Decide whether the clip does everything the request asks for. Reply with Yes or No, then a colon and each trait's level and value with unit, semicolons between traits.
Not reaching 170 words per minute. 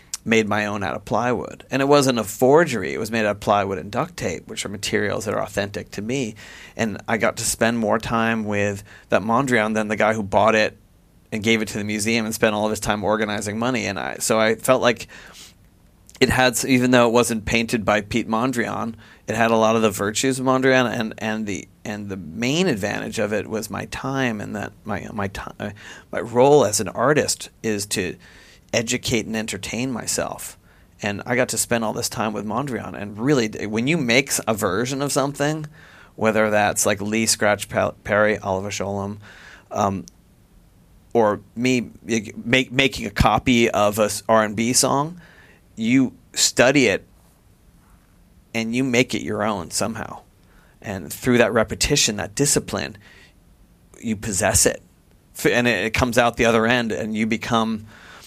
No: average, 185 wpm